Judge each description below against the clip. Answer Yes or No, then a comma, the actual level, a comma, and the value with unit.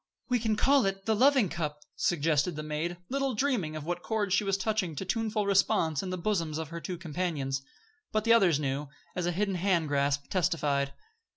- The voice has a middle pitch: Yes, medium, 175 Hz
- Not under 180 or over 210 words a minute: Yes, average, 195 wpm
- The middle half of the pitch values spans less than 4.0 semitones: No, average, 5.3 semitones